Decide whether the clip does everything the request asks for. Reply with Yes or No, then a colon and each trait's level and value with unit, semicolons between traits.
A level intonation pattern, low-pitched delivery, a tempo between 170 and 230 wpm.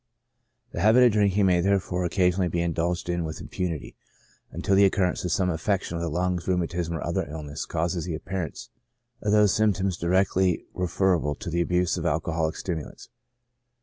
Yes: narrow, 2.3 semitones; very low, 90 Hz; average, 180 wpm